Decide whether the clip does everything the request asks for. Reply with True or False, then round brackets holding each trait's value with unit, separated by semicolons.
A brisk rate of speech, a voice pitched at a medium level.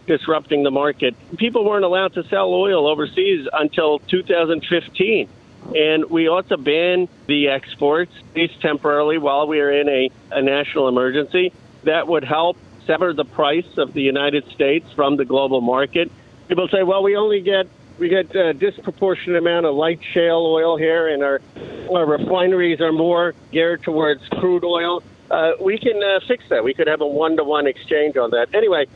False (175 wpm; 165 Hz)